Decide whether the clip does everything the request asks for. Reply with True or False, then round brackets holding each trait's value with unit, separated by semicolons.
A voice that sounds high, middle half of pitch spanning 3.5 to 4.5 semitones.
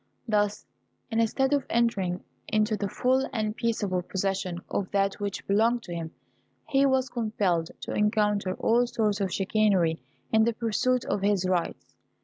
False (210 Hz; 3.1 semitones)